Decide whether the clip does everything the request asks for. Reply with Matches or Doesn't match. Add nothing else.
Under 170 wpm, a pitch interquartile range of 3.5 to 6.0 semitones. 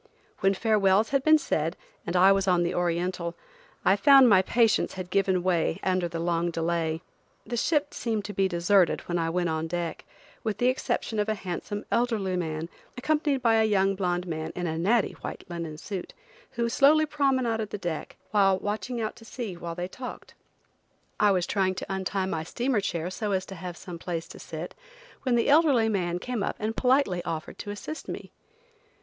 Doesn't match